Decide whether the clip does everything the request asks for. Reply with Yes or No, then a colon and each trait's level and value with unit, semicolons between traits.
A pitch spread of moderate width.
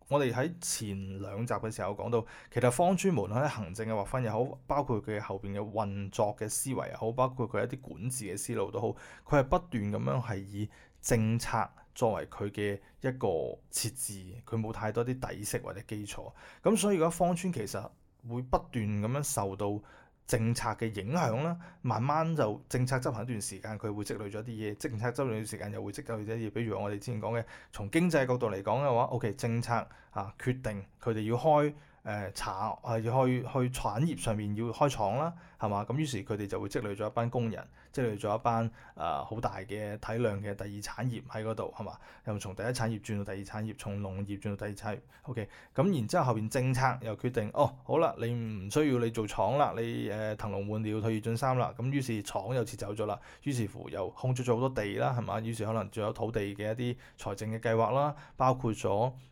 Yes: average, 3.3 semitones